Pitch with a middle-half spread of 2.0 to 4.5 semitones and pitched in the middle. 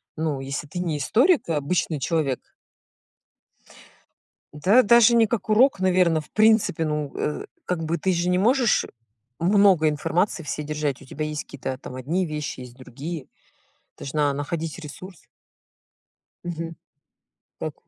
Yes: average, 4.0 semitones; medium, 165 Hz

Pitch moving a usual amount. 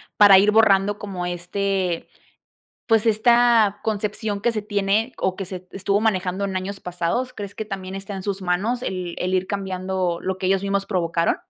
No: narrow, 2.0 semitones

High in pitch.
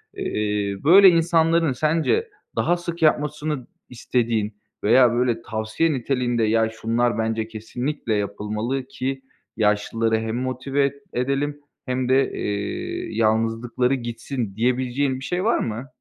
No: low, 125 Hz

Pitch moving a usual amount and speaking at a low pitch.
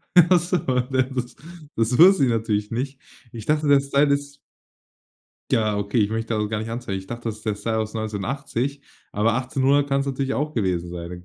Yes: average, 4.5 semitones; low, 120 Hz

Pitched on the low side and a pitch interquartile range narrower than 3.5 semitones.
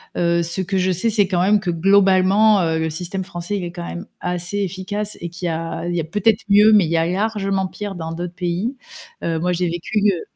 No: medium, 185 Hz; average, 2.8 semitones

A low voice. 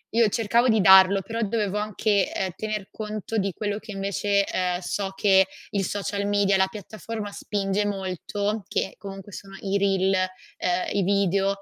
No: high, 200 Hz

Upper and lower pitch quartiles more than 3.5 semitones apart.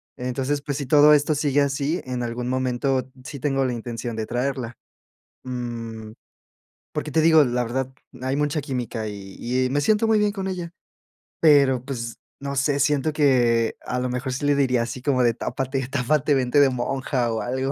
No: average, 2.8 semitones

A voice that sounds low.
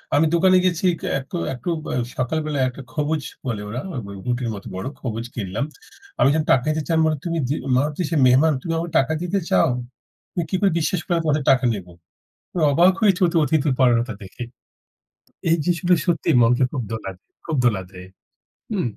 No: medium, 150 Hz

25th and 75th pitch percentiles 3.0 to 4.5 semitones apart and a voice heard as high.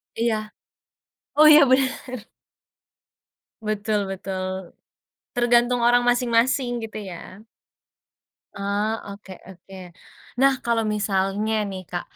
Yes: average, 3.8 semitones; high, 215 Hz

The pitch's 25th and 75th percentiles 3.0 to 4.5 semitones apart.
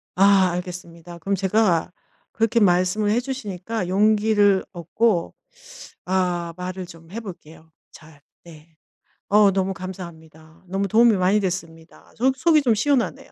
Yes: average, 3.7 semitones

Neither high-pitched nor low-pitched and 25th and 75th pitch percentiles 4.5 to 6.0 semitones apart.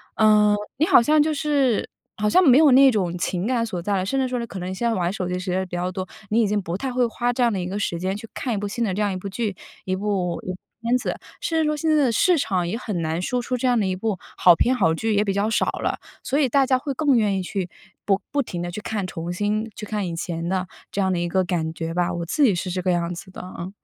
No: high, 205 Hz; average, 5.0 semitones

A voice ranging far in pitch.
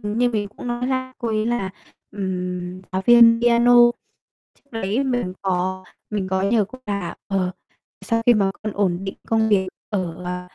No: average, 4.0 semitones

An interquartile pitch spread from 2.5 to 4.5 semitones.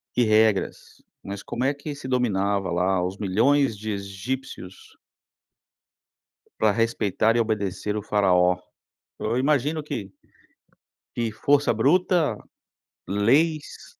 No: average, 5.1 semitones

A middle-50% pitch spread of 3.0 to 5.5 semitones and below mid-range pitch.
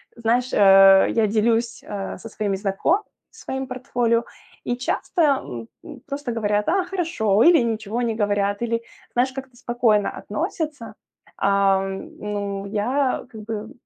No: average, 3.9 semitones; high, 225 Hz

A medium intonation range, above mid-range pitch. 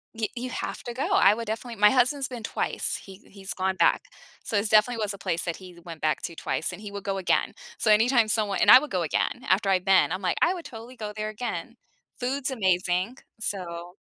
Yes: average, 4.2 semitones; high, 210 Hz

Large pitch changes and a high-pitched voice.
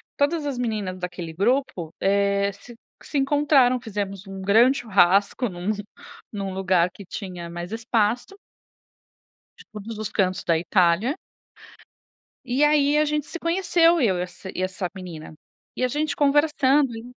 Yes: wide, 6.7 semitones; high, 215 Hz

